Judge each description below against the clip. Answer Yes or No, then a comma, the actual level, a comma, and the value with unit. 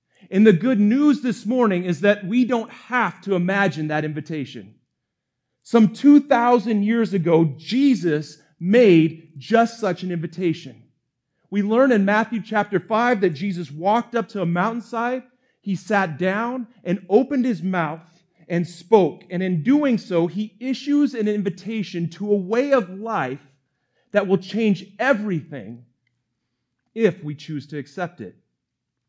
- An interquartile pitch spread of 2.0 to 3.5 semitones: No, wide, 5.4 semitones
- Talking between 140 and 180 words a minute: Yes, average, 145 wpm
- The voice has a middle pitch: No, high, 195 Hz